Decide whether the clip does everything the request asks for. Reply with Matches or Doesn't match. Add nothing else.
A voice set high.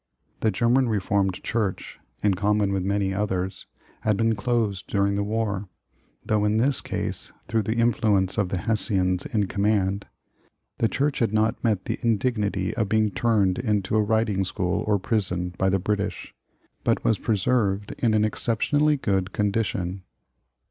Doesn't match